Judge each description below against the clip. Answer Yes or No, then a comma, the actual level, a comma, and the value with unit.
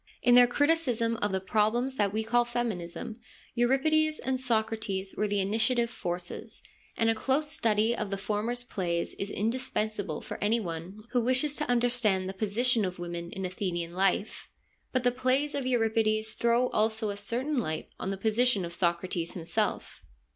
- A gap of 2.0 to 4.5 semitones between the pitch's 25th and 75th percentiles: Yes, average, 4.1 semitones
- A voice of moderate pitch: No, high, 220 Hz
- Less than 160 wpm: No, average, 170 wpm